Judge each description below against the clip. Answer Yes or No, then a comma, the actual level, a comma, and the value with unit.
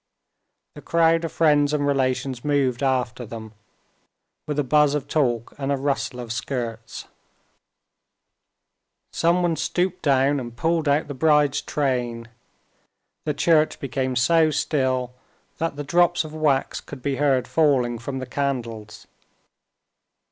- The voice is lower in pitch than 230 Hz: Yes, medium, 140 Hz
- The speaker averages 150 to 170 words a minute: No, slow, 135 wpm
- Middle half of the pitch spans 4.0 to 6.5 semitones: No, average, 3.3 semitones